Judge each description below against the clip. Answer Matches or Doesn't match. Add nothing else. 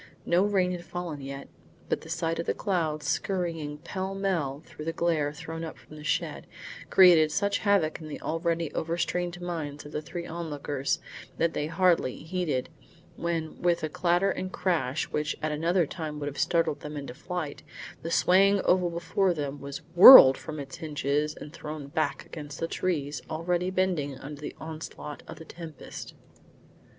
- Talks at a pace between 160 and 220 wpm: Matches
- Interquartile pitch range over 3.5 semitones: Doesn't match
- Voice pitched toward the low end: Doesn't match